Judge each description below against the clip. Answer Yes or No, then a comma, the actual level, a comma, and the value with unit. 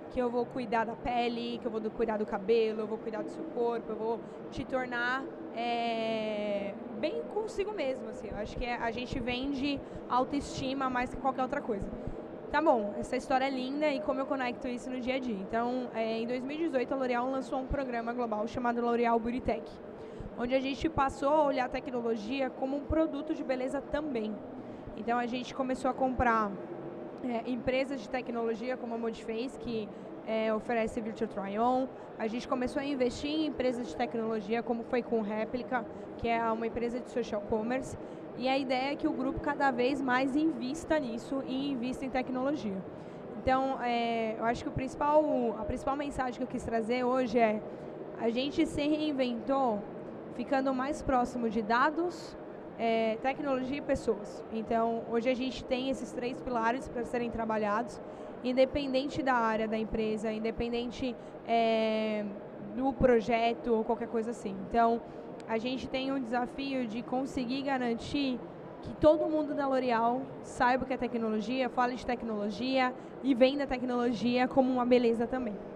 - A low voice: No, high, 245 Hz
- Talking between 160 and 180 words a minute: Yes, average, 175 wpm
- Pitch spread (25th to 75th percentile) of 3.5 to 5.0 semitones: No, narrow, 2.6 semitones